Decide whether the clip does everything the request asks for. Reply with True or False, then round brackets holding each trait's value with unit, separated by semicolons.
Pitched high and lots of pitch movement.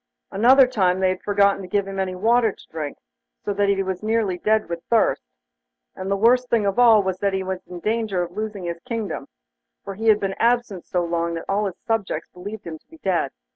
False (195 Hz; 3.1 semitones)